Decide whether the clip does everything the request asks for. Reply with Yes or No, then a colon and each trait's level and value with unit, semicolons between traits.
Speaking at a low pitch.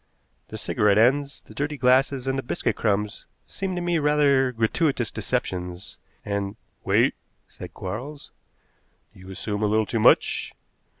Yes: low, 120 Hz